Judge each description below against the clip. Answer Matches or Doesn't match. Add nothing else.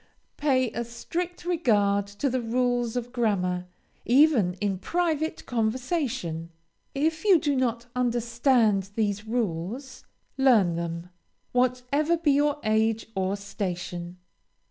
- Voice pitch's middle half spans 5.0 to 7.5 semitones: Matches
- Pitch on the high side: Matches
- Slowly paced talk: Matches